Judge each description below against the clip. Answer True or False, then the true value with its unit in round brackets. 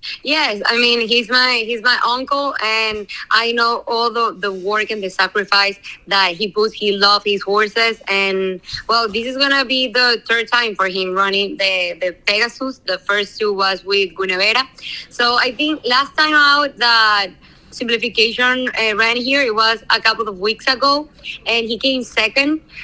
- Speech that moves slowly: False (180 wpm)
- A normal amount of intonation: True (3.6 semitones)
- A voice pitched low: False (225 Hz)